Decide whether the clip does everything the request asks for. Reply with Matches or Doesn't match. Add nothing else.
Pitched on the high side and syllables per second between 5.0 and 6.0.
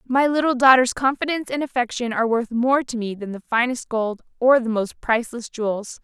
Matches